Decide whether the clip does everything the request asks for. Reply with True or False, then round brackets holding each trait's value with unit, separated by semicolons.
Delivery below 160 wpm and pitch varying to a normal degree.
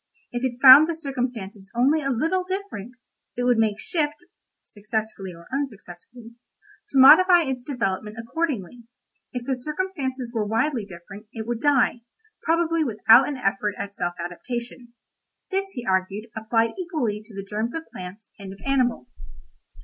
True (150 wpm; 5.0 semitones)